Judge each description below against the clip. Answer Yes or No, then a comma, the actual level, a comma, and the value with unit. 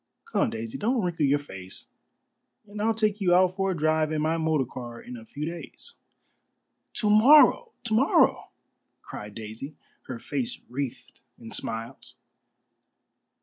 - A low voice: No, medium, 155 Hz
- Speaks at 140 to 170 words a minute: Yes, average, 145 wpm